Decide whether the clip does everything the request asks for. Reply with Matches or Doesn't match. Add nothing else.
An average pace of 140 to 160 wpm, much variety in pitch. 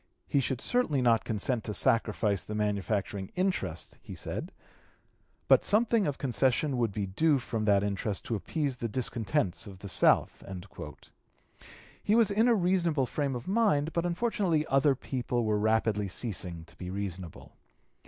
Matches